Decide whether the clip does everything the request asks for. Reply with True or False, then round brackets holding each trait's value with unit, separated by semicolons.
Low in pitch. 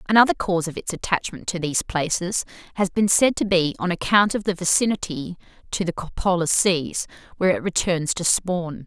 False (180 Hz)